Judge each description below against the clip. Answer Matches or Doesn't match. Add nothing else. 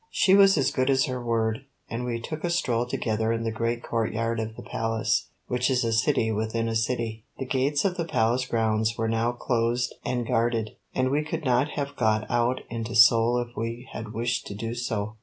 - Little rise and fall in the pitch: Matches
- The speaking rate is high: Matches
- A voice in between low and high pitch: Doesn't match